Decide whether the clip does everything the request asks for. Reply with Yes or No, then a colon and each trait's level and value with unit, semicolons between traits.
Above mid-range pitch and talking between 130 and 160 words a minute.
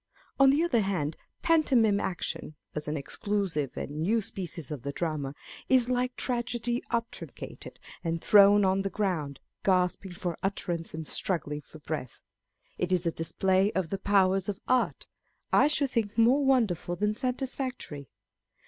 Yes: high, 195 Hz; average, 150 wpm